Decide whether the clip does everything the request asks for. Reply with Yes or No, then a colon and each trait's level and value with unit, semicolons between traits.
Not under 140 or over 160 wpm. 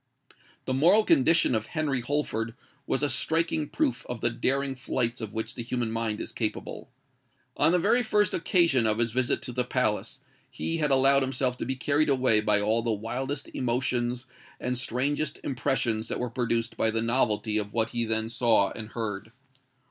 No: average, 185 wpm